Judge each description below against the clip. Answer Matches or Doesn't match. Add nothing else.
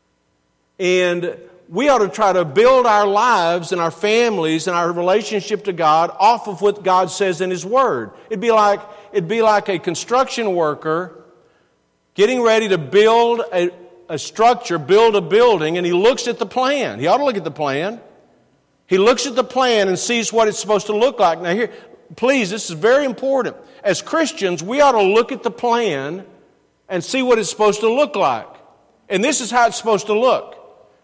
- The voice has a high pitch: Matches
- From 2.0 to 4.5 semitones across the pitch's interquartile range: Doesn't match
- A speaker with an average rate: Matches